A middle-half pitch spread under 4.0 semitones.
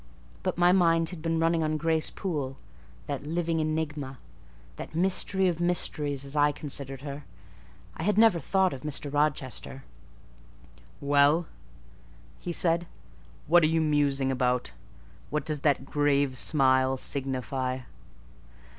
Yes: average, 3.2 semitones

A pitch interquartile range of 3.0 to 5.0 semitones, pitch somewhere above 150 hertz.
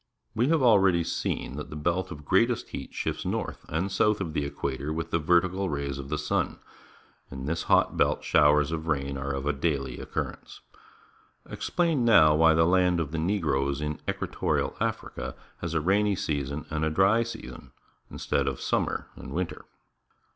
No: average, 4.7 semitones; very low, 80 Hz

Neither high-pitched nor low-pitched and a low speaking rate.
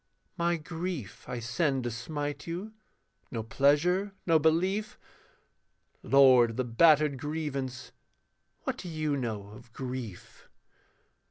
Yes: medium, 145 Hz; slow, 115 wpm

